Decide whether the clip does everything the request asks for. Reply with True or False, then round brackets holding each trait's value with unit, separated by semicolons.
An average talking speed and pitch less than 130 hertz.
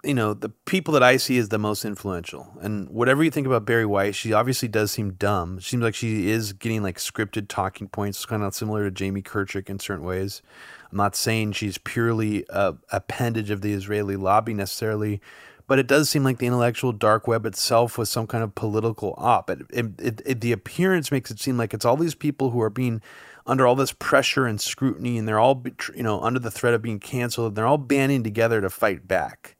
False (230 wpm; 115 Hz)